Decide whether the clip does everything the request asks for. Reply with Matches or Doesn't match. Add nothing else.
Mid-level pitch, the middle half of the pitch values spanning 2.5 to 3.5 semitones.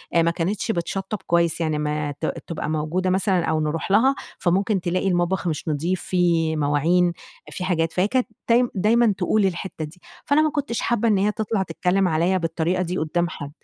Matches